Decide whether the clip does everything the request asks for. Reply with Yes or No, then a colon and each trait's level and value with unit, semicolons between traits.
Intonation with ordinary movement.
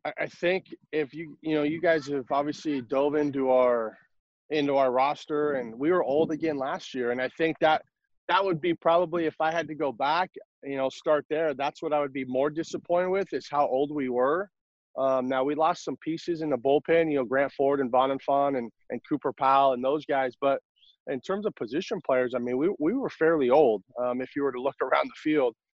Yes: average, 3.3 semitones